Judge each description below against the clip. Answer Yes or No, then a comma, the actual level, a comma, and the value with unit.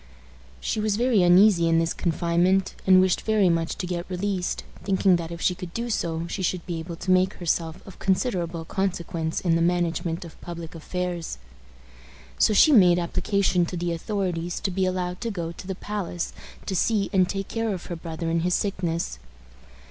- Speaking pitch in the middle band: Yes, medium, 180 Hz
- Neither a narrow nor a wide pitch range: No, narrow, 2.3 semitones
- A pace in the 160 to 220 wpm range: Yes, average, 190 wpm